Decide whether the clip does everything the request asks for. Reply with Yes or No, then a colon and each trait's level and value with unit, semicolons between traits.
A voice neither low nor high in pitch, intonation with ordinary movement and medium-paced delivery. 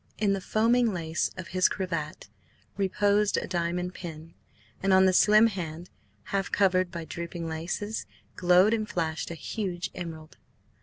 Yes: medium, 180 Hz; average, 3.1 semitones; average, 150 wpm